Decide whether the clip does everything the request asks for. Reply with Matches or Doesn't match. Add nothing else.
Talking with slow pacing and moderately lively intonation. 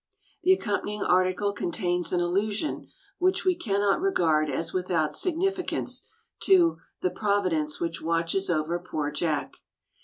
Matches